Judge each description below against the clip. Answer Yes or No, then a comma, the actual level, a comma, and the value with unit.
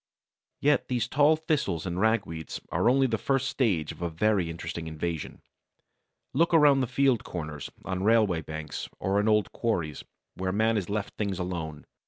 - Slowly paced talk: No, average, 170 wpm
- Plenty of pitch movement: Yes, wide, 6.7 semitones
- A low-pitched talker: Yes, low, 100 Hz